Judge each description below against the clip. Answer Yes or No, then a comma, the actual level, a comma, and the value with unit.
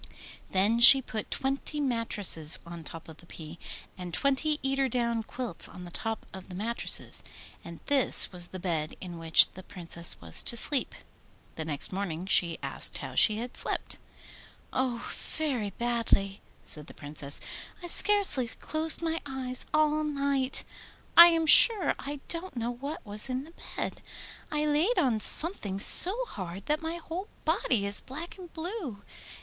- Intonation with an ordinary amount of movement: No, wide, 8.2 semitones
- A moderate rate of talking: Yes, average, 165 wpm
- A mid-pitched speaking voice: No, high, 240 Hz